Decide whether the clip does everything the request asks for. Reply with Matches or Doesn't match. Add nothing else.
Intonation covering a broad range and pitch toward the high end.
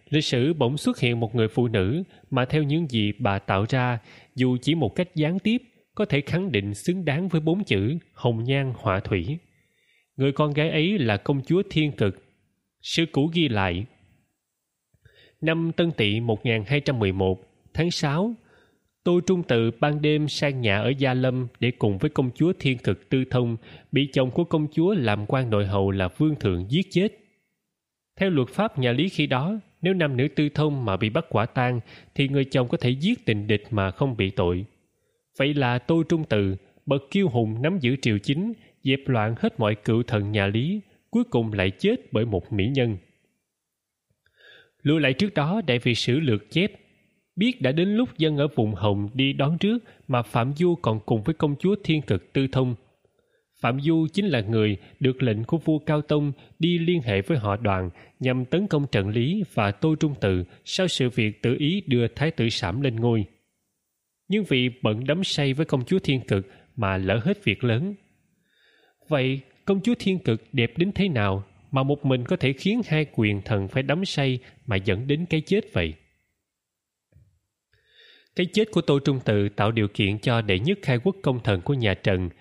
Doesn't match